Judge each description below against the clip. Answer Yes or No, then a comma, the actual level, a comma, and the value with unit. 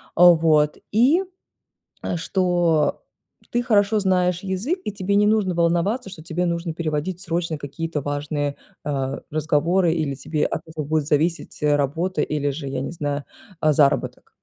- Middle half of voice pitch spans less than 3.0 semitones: No, average, 3.8 semitones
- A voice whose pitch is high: No, medium, 165 Hz